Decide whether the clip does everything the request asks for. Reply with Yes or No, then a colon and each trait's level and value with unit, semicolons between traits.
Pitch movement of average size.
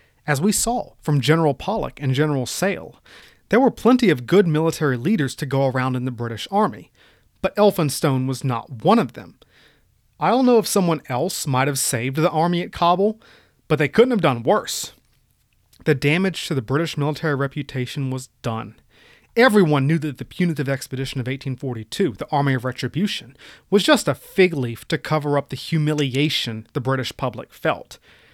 Yes: average, 4.7 semitones